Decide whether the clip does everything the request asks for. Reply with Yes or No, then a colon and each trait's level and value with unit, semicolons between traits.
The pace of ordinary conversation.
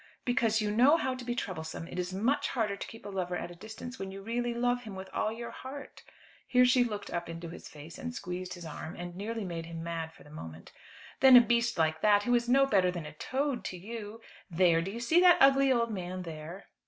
No: fast, 245 wpm